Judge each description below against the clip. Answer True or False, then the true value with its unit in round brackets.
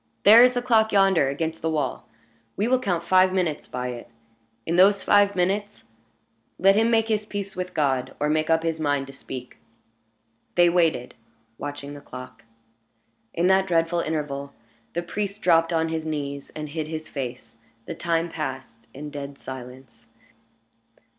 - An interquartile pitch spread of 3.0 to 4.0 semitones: False (5.1 semitones)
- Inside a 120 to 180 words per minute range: True (165 wpm)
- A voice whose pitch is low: False (160 Hz)